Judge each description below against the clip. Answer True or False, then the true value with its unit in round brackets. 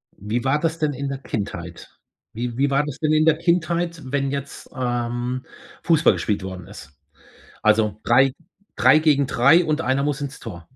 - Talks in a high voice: False (135 Hz)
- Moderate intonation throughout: True (4.4 semitones)